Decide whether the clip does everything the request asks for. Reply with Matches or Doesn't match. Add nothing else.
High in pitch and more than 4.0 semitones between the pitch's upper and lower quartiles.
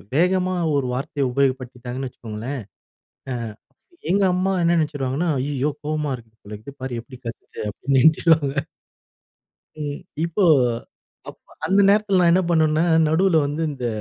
Doesn't match